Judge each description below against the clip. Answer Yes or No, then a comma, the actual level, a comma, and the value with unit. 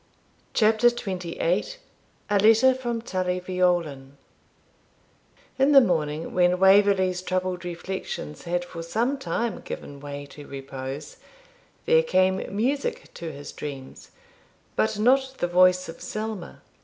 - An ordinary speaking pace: No, slow, 120 wpm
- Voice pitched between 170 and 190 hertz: Yes, medium, 185 Hz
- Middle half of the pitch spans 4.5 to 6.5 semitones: Yes, average, 4.8 semitones